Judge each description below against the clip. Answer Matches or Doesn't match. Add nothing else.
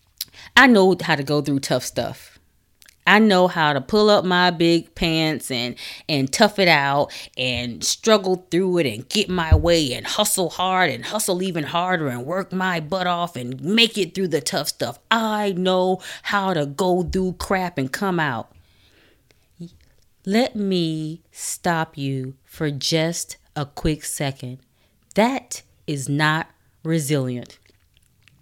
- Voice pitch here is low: Doesn't match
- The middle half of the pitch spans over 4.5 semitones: Matches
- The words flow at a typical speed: Matches